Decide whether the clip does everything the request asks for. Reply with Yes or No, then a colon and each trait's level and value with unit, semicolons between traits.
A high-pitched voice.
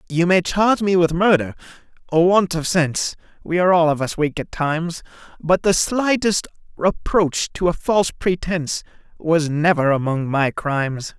No: medium, 165 Hz